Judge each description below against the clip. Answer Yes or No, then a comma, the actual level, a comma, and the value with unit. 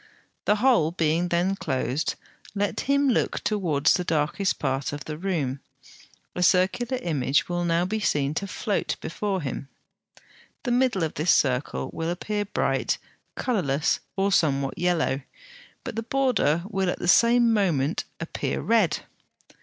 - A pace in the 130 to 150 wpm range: Yes, average, 145 wpm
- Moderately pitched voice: Yes, medium, 175 Hz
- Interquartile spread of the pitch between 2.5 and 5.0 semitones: No, wide, 5.4 semitones